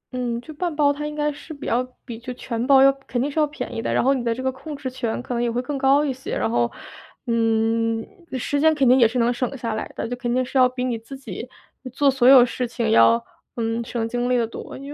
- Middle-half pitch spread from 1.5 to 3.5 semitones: Yes, average, 2.8 semitones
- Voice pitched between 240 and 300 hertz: Yes, very high, 250 Hz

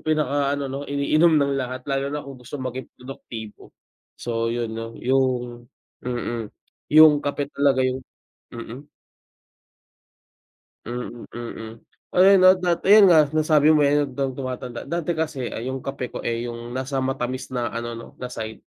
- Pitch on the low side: Yes, low, 130 Hz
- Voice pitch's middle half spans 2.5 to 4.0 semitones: Yes, average, 3.2 semitones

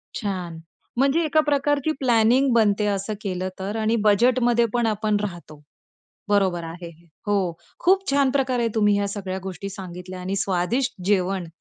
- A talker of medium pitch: No, high, 205 Hz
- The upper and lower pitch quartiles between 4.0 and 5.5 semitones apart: Yes, average, 4.7 semitones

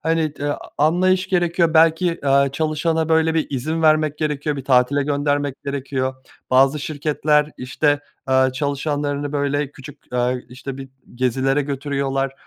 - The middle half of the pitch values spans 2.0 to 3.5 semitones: Yes, narrow, 2.4 semitones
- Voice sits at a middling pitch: Yes, medium, 145 Hz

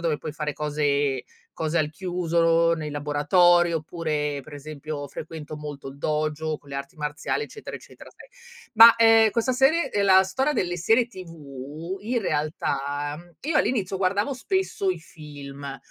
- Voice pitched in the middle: Yes, medium, 160 Hz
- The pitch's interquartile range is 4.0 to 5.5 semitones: Yes, average, 4.4 semitones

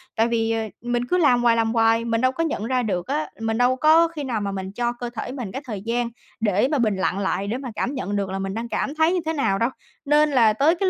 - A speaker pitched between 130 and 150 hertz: No, high, 235 Hz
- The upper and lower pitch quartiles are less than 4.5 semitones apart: Yes, average, 3.6 semitones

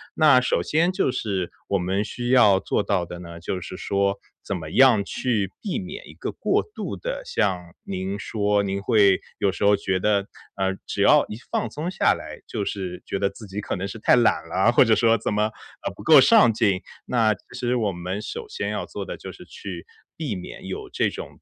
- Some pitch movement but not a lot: Yes, average, 4.0 semitones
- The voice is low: Yes, low, 100 Hz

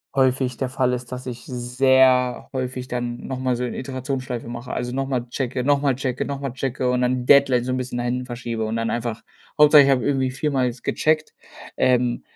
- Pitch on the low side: Yes, low, 125 Hz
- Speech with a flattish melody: Yes, narrow, 1.4 semitones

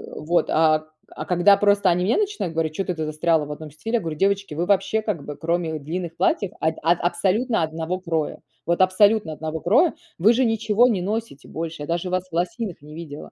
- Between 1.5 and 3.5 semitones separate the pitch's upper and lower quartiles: No, average, 4.1 semitones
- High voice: No, medium, 175 Hz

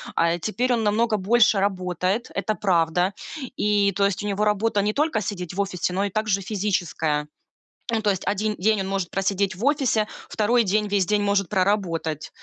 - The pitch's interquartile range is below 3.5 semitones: Yes, narrow, 2.5 semitones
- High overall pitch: Yes, high, 200 Hz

